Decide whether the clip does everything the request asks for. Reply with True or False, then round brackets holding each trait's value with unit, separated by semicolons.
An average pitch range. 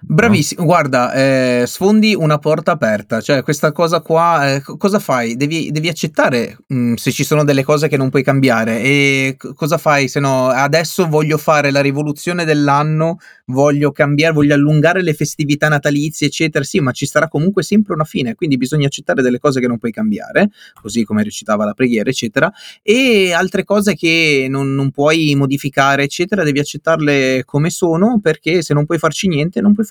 True (3.5 semitones)